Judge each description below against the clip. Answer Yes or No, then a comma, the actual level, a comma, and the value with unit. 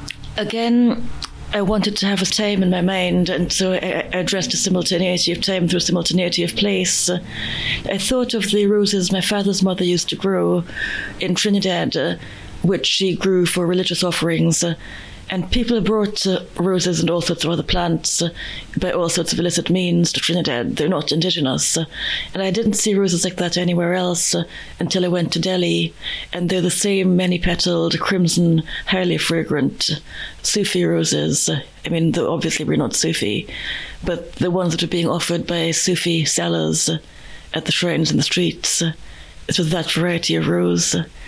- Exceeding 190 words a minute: No, average, 170 wpm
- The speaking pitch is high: No, medium, 175 Hz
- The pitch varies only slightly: Yes, narrow, 2.0 semitones